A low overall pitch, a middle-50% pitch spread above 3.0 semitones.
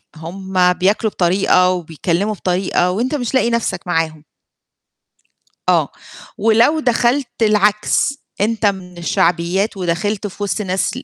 No: high, 195 Hz; average, 3.5 semitones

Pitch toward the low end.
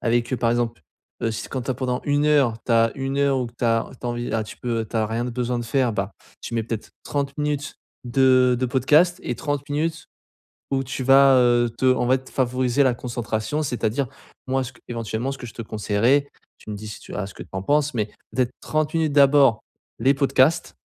Yes: low, 125 Hz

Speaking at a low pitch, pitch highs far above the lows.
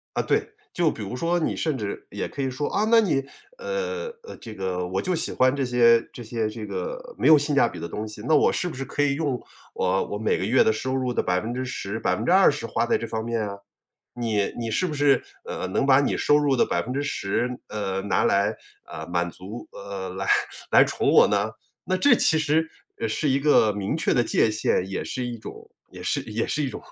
Yes: low, 120 Hz; wide, 5.8 semitones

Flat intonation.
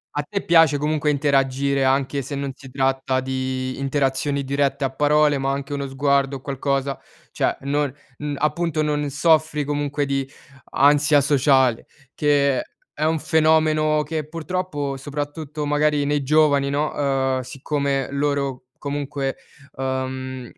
Yes: narrow, 1.6 semitones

